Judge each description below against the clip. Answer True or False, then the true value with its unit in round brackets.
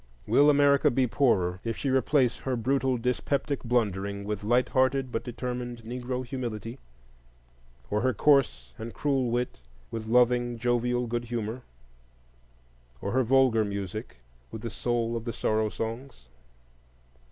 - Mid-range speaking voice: False (120 Hz)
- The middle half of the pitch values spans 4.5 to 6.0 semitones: False (2.5 semitones)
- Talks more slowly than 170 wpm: True (140 wpm)